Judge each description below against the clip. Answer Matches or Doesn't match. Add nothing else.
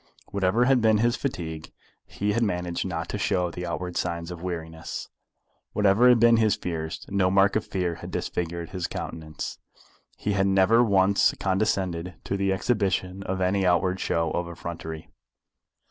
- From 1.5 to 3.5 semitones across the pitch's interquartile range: Matches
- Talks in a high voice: Doesn't match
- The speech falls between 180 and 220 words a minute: Doesn't match